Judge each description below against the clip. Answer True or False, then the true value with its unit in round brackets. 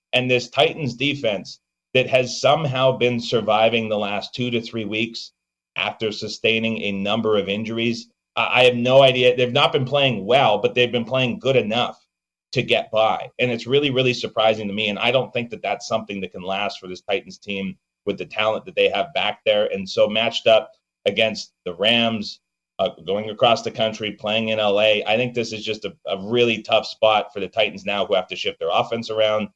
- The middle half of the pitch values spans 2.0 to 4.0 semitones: True (2.9 semitones)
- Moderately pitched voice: False (115 Hz)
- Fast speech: True (210 wpm)